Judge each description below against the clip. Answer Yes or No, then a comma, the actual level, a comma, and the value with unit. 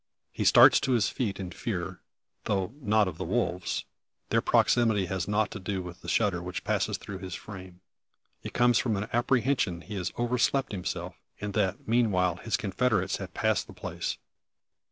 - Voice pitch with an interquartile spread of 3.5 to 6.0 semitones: Yes, average, 3.8 semitones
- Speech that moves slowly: No, average, 175 wpm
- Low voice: Yes, low, 100 Hz